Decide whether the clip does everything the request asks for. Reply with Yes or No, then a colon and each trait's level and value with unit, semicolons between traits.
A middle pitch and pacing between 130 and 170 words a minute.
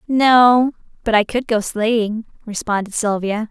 No: high, 225 Hz; slow, 135 wpm